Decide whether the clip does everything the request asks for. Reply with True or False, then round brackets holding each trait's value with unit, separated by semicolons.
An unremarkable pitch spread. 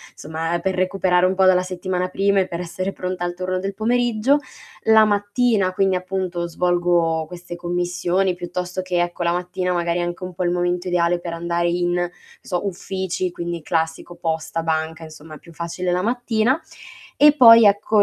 False (1.7 semitones)